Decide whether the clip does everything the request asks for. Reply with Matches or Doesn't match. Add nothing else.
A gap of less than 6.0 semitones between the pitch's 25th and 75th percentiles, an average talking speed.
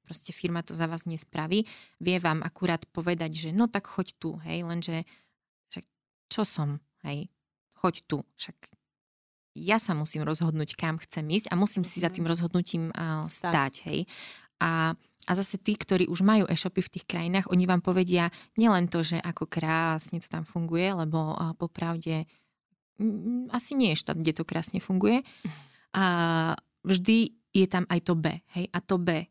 Doesn't match